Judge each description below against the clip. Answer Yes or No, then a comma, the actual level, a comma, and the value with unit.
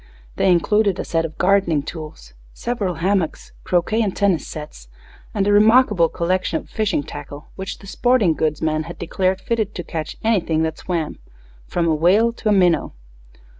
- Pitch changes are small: No, average, 4.2 semitones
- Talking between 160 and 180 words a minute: Yes, average, 170 wpm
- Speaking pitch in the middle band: Yes, medium, 180 Hz